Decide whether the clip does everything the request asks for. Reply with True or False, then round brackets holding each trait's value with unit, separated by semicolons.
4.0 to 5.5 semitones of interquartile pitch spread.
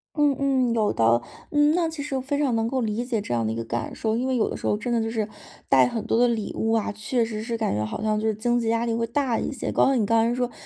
False (2.9 semitones)